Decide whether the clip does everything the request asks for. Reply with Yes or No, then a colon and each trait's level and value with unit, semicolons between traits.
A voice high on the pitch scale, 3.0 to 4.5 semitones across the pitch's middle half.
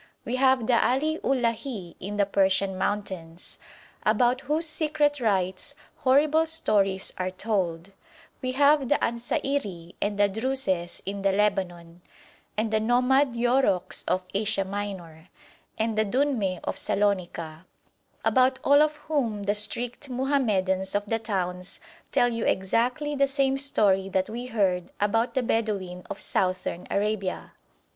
No: high, 215 Hz; wide, 5.4 semitones